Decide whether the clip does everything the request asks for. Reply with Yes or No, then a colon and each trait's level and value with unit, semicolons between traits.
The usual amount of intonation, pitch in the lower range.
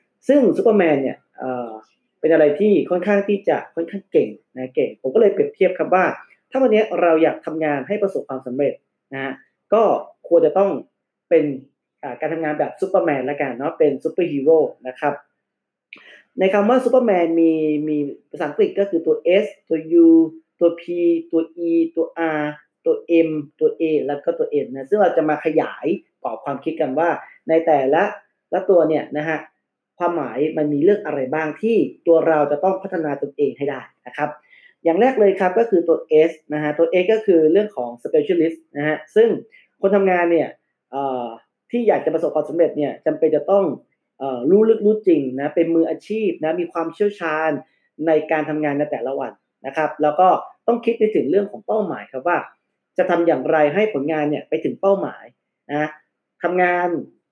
No: average, 4.9 semitones; medium, 165 Hz